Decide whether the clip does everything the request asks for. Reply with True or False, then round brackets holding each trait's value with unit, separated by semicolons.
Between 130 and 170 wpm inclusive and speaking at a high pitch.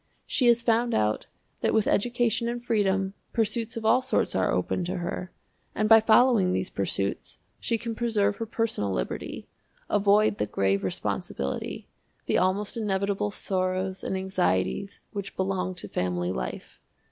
True (150 wpm; 200 Hz)